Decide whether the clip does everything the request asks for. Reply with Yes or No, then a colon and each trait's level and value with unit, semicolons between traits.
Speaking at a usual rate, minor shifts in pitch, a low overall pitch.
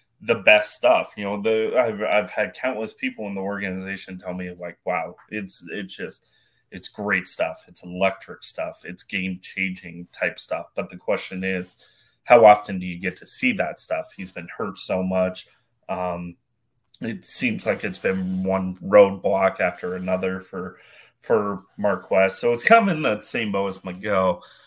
Yes: average, 180 wpm; narrow, 1.9 semitones; very low, 95 Hz